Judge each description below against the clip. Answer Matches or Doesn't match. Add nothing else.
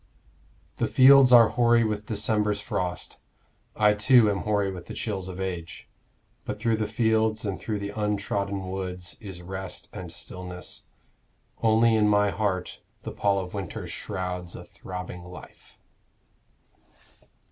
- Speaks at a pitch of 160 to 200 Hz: Doesn't match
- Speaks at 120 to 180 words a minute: Matches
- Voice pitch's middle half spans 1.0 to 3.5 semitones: Matches